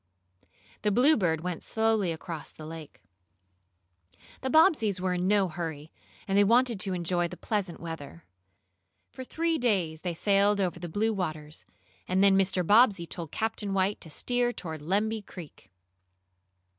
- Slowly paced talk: No, average, 150 wpm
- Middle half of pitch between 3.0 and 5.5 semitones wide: Yes, average, 4.3 semitones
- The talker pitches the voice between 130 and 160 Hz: No, high, 190 Hz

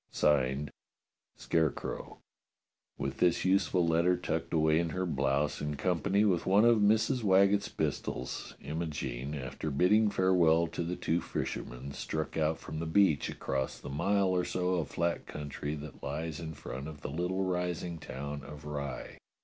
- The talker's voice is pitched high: No, very low, 80 Hz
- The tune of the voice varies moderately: Yes, average, 3.9 semitones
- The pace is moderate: Yes, average, 155 wpm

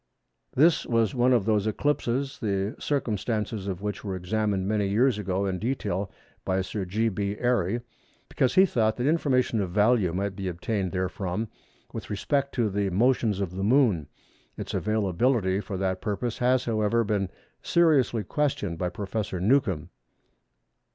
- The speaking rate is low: No, average, 155 wpm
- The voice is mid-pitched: No, low, 105 Hz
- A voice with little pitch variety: No, average, 4.1 semitones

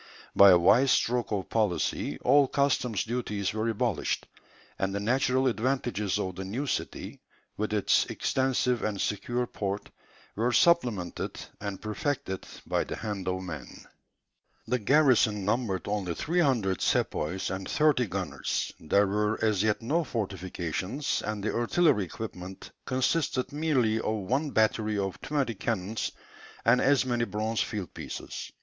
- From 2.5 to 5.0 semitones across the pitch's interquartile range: Yes, average, 4.5 semitones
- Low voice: Yes, low, 110 Hz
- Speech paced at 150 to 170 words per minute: No, average, 140 wpm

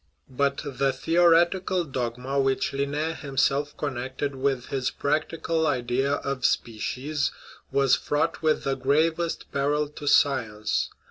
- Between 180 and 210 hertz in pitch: No, medium, 140 Hz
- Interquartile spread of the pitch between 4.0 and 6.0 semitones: No, narrow, 2.6 semitones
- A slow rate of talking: Yes, slow, 125 wpm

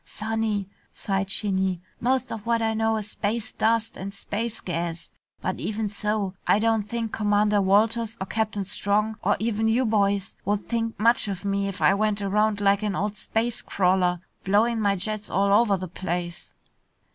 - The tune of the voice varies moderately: No, narrow, 2.1 semitones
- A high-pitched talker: Yes, high, 210 Hz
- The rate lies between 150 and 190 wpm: Yes, average, 175 wpm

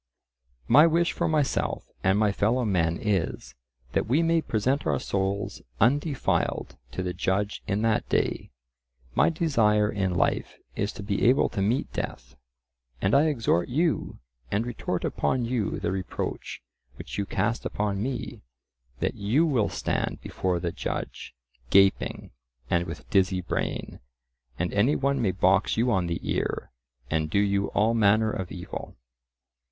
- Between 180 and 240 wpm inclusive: No, average, 150 wpm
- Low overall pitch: Yes, low, 105 Hz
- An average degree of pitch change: Yes, average, 4.7 semitones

